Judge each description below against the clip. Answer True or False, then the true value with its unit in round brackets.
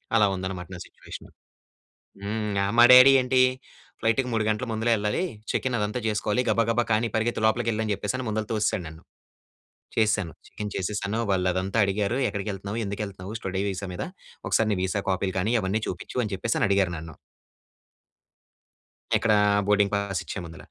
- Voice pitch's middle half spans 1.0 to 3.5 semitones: True (2.6 semitones)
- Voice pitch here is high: False (105 Hz)